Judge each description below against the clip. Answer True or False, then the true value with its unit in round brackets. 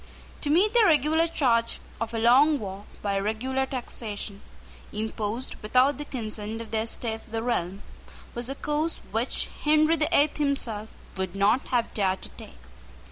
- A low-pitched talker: False (235 Hz)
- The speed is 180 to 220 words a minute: False (165 wpm)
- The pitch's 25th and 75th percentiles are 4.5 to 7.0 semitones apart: True (5.1 semitones)